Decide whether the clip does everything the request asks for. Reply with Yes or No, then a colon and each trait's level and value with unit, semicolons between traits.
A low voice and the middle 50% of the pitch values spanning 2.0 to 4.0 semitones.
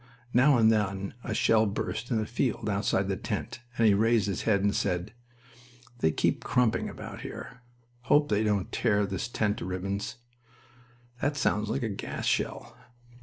Yes: low, 110 Hz; average, 3.2 semitones